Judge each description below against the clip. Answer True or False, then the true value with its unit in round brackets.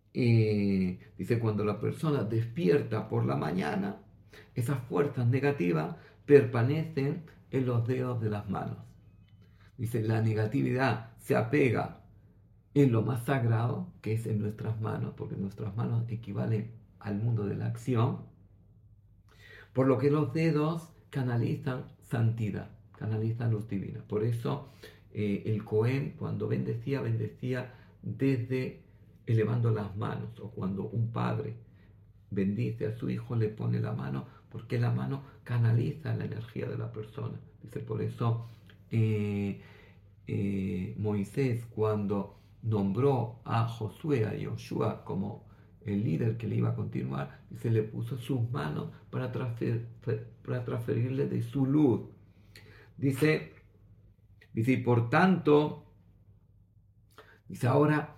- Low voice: True (110 Hz)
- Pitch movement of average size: True (3.6 semitones)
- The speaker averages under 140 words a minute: True (125 wpm)